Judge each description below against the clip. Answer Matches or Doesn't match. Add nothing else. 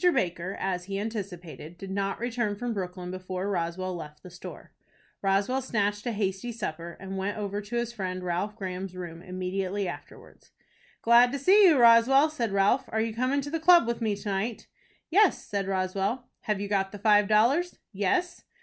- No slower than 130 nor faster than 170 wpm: Doesn't match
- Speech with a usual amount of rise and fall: Matches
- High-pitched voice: Matches